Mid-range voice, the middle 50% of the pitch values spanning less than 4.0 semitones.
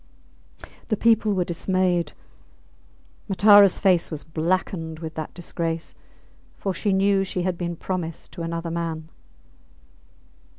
Yes: medium, 175 Hz; narrow, 2.6 semitones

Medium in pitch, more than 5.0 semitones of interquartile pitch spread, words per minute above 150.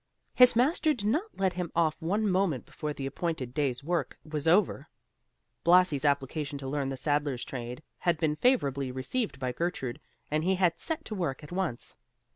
Yes: medium, 155 Hz; wide, 5.4 semitones; average, 180 wpm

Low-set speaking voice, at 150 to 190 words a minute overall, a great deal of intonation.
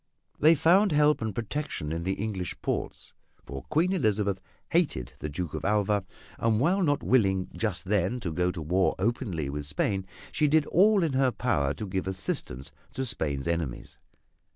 Yes: low, 100 Hz; average, 175 wpm; wide, 8.6 semitones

